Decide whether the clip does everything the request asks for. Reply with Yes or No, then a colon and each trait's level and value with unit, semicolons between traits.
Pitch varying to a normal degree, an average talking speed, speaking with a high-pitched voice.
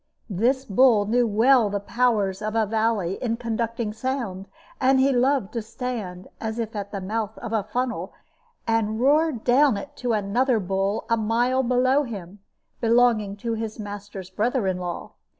Yes: average, 3.3 semitones; average, 170 wpm; high, 225 Hz